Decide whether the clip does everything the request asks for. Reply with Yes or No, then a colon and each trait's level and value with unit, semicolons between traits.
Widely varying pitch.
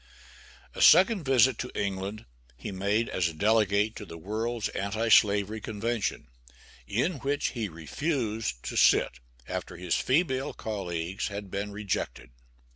No: average, 3.3 semitones